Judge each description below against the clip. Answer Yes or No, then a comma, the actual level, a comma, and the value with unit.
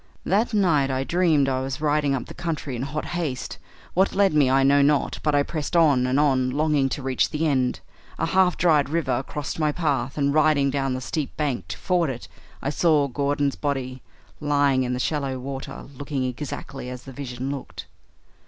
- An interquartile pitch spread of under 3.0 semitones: Yes, narrow, 2.5 semitones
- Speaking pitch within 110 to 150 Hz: Yes, medium, 140 Hz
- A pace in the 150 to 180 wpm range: No, average, 200 wpm